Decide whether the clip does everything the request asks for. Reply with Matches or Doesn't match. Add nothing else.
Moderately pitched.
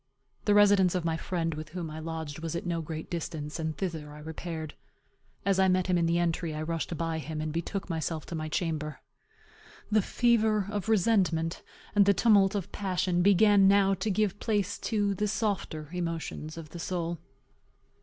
Matches